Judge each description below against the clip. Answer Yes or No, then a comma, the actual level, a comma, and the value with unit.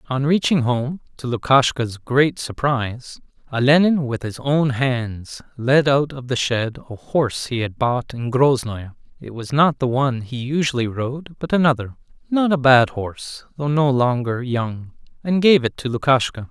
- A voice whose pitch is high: No, low, 130 Hz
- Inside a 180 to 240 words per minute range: No, average, 165 wpm